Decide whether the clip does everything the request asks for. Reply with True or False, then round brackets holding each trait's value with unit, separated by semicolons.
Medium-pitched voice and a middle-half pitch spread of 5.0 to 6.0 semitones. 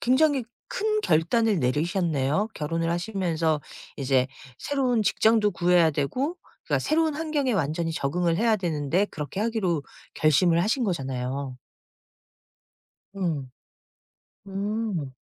False (175 Hz; 6.6 semitones)